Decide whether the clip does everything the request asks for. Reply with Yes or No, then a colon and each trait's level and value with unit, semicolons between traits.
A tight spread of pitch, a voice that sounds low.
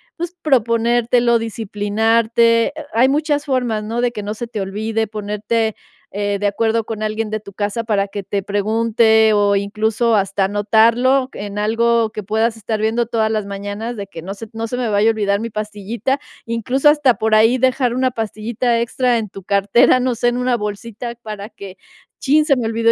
No: narrow, 2.3 semitones; high, 225 Hz